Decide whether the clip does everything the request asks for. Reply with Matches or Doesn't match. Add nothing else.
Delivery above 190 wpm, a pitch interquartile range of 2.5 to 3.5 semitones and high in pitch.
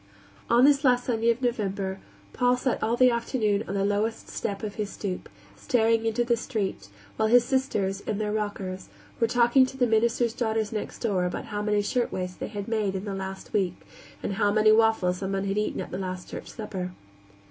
Matches